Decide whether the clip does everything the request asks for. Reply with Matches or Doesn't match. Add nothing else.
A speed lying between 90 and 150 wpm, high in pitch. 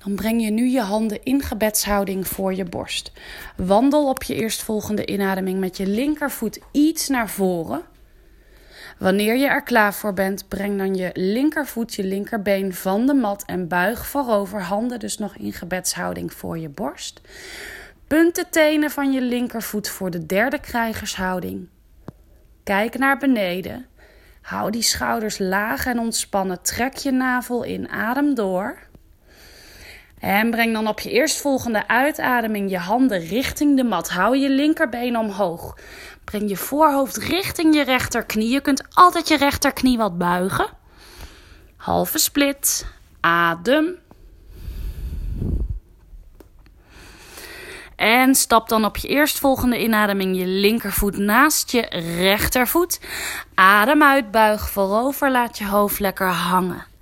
Matches